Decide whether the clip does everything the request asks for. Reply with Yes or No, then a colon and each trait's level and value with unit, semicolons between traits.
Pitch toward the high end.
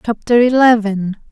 Yes: high, 225 Hz